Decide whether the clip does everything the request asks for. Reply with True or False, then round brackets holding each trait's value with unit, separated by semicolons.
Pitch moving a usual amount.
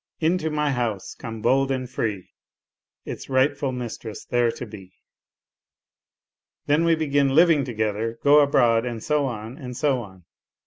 True (4.2 semitones)